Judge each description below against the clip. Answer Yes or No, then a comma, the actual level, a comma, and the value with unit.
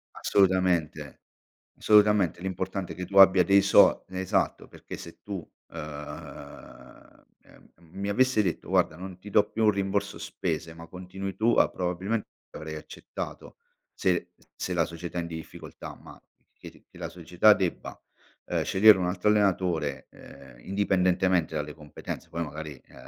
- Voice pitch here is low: Yes, very low, 90 Hz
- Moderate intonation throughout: Yes, average, 3.2 semitones